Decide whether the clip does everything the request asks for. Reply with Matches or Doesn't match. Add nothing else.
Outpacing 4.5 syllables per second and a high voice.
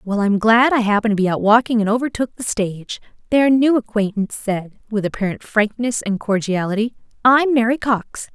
Matches